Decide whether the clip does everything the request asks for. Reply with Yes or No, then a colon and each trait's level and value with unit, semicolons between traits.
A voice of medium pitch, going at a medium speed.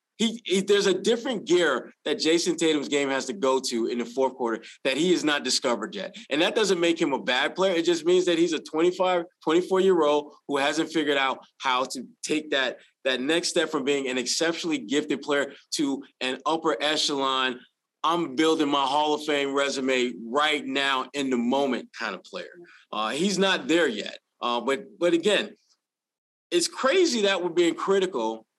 Yes: medium, 155 Hz; average, 190 wpm